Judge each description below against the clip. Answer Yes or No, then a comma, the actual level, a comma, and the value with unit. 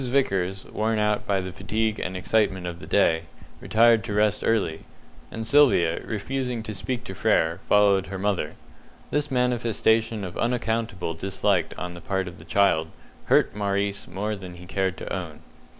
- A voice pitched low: Yes, low, 100 Hz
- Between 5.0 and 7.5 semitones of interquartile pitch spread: No, average, 3.3 semitones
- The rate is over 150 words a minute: Yes, average, 165 wpm